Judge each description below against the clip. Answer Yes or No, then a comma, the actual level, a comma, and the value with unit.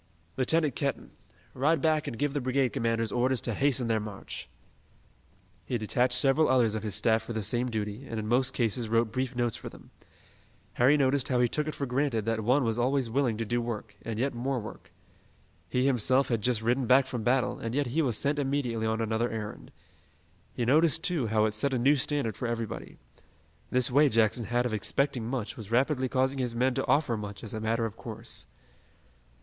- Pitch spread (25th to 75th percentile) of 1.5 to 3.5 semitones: Yes, average, 3.1 semitones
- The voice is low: Yes, low, 120 Hz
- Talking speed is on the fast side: Yes, fast, 210 wpm